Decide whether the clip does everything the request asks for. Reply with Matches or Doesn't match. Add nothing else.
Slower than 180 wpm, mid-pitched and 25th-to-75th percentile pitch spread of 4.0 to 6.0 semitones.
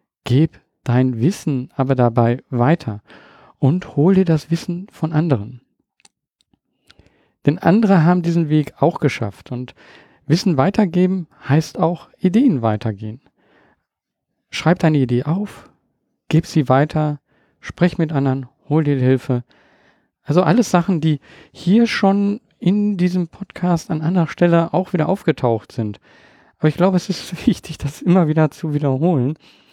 Matches